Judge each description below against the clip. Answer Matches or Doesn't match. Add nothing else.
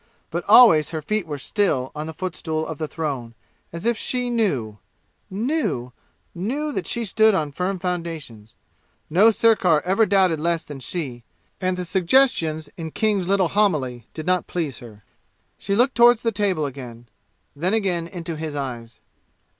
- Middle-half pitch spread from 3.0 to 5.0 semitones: Doesn't match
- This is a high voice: Doesn't match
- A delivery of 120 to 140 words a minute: Doesn't match